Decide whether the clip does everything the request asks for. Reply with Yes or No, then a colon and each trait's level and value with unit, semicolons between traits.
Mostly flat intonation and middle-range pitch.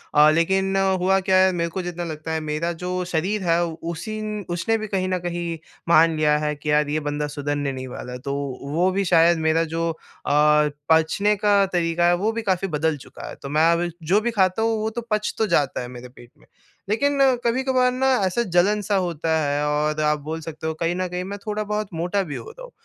No: average, 4.6 semitones; medium, 170 Hz